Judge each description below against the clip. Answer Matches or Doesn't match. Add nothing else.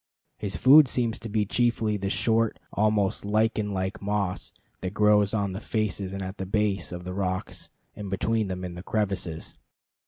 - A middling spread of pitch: Doesn't match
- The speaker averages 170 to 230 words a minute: Matches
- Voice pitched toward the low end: Matches